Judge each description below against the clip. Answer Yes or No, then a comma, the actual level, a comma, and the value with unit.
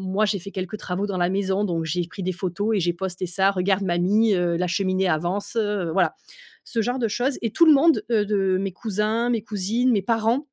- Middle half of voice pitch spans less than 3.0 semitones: No, average, 3.3 semitones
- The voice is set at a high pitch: Yes, high, 195 Hz